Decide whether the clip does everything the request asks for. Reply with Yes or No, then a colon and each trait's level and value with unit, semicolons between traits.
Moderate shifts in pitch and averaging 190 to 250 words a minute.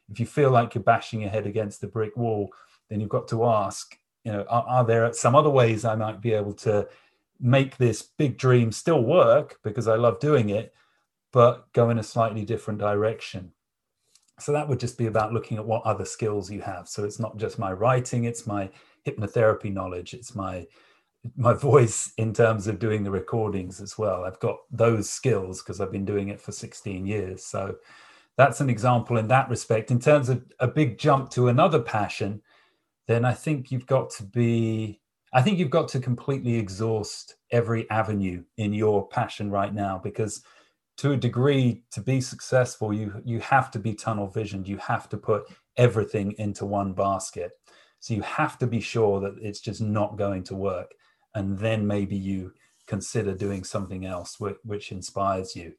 Yes: average, 3.0 semitones; average, 195 wpm